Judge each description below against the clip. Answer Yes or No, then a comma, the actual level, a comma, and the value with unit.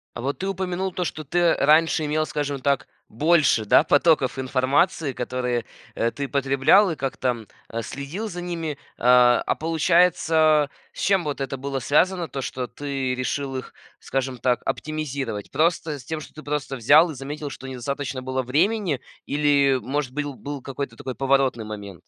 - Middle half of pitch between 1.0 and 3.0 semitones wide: No, average, 3.4 semitones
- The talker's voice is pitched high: No, medium, 140 Hz